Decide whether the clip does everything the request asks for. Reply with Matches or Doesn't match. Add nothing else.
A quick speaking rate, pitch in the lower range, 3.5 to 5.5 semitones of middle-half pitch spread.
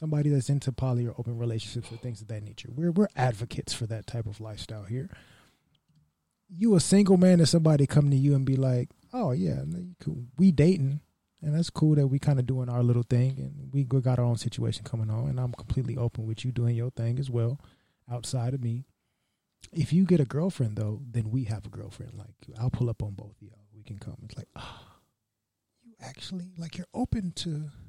Matches